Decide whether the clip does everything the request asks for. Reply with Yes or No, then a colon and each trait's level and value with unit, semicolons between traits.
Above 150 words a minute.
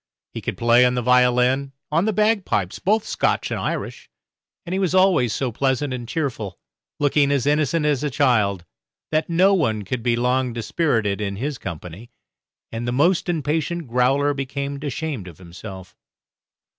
Yes: average, 165 wpm